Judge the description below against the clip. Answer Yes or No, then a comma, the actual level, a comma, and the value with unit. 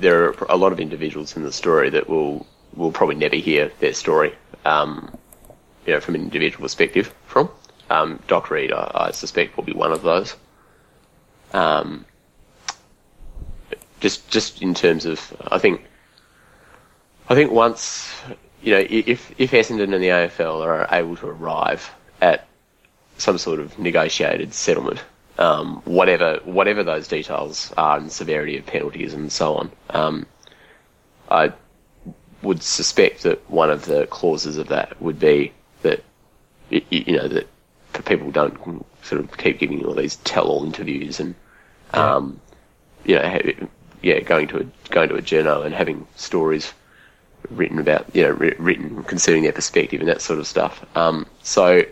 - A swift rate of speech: No, average, 155 wpm